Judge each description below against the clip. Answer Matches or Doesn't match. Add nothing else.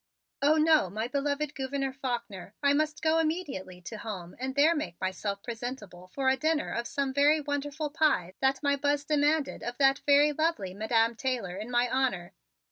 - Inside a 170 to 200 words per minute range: Matches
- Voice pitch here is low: Doesn't match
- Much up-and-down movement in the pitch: Doesn't match